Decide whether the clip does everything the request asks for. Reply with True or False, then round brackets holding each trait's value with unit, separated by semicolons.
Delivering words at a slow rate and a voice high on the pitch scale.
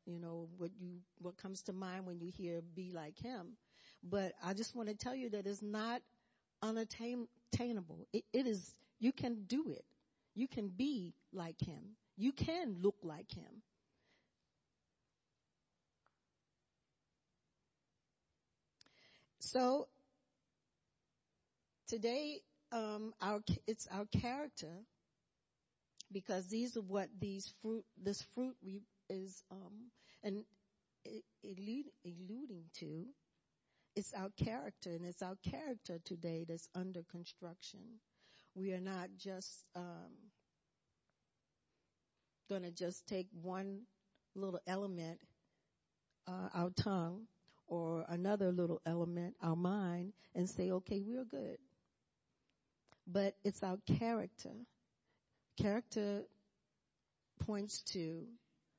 True (110 wpm; 195 Hz)